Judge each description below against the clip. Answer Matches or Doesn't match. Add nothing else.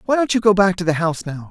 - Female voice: Doesn't match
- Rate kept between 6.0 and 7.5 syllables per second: Matches